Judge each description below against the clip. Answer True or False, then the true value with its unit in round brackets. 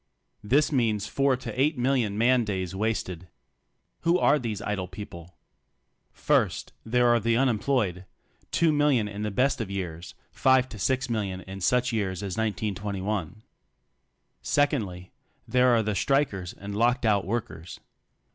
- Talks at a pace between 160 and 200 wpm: False (145 wpm)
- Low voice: True (110 Hz)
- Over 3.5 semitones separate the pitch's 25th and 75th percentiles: True (4.7 semitones)